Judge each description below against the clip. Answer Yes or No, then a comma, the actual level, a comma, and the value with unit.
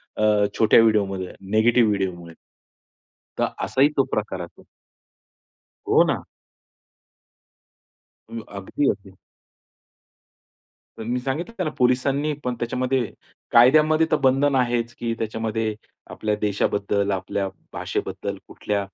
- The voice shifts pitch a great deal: No, average, 4.2 semitones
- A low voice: Yes, low, 115 Hz